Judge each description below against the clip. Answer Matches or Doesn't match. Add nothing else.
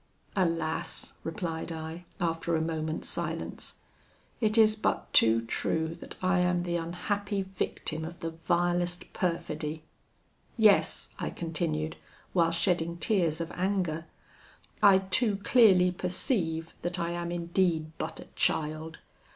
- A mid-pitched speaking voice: Matches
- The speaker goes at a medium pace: Doesn't match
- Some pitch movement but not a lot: Doesn't match